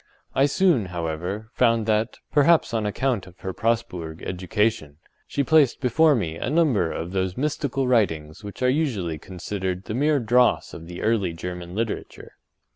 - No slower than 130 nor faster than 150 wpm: No, average, 160 wpm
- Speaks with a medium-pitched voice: No, low, 105 Hz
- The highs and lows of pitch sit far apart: Yes, wide, 6.2 semitones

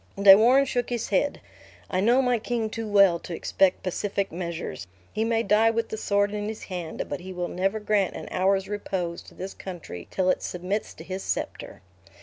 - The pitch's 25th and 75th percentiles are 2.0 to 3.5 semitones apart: Yes, average, 3.1 semitones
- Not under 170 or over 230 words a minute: Yes, average, 200 wpm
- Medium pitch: No, high, 200 Hz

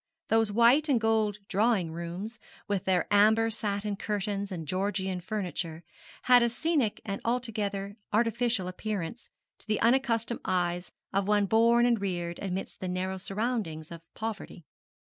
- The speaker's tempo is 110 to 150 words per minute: Yes, average, 145 wpm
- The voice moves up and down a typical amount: Yes, average, 3.5 semitones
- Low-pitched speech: No, high, 205 Hz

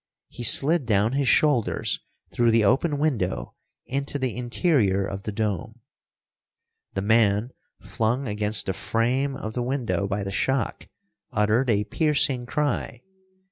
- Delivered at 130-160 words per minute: Yes, average, 140 wpm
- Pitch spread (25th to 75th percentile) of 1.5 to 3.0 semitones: No, average, 4.6 semitones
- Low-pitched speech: Yes, low, 120 Hz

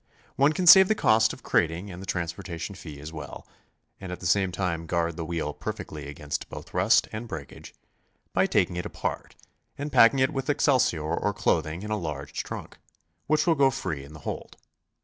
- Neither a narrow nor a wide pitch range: No, wide, 6.7 semitones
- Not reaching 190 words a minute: No, average, 195 wpm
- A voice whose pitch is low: Yes, very low, 90 Hz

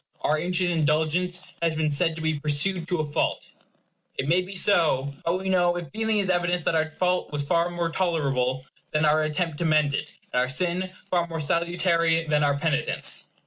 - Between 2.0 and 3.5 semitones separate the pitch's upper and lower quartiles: Yes, average, 2.7 semitones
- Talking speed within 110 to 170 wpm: No, average, 195 wpm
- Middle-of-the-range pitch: Yes, medium, 165 Hz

